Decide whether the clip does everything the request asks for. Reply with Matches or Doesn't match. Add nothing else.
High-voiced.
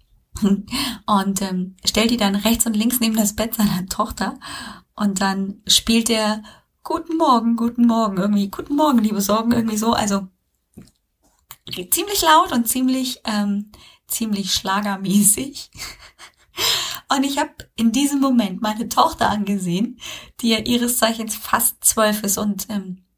Matches